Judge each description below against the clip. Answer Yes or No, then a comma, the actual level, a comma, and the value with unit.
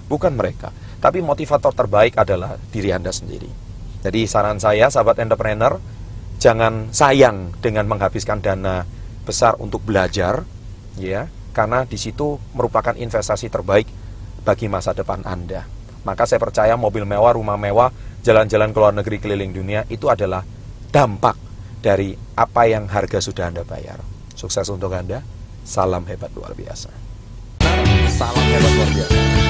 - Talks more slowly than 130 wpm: No, average, 135 wpm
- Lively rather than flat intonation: No, narrow, 2.5 semitones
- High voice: No, low, 105 Hz